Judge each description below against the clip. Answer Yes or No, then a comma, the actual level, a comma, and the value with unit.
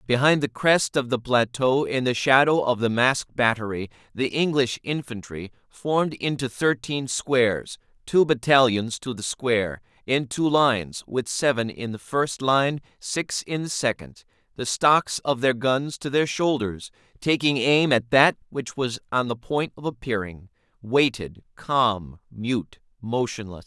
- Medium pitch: No, low, 125 Hz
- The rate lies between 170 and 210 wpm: No, average, 155 wpm